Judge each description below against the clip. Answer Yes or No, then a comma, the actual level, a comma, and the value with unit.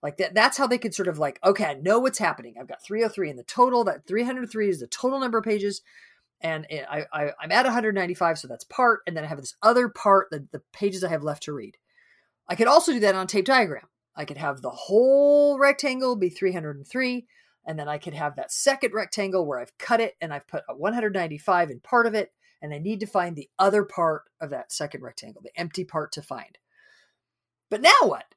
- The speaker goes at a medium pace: No, fast, 235 wpm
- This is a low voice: No, high, 195 Hz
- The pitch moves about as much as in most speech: No, wide, 7.4 semitones